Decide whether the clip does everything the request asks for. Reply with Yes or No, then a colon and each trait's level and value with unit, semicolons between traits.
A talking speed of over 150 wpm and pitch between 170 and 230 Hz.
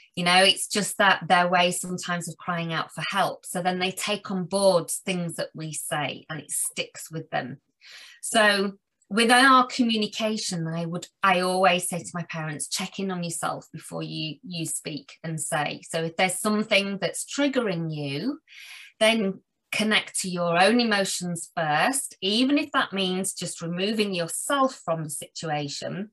Yes: average, 170 wpm; medium, 185 Hz